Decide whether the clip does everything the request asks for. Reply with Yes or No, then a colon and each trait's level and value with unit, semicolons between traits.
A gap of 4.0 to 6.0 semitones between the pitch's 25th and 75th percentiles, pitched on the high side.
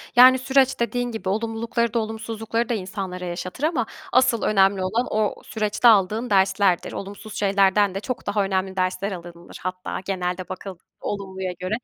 No: average, 3.3 semitones; high, 205 Hz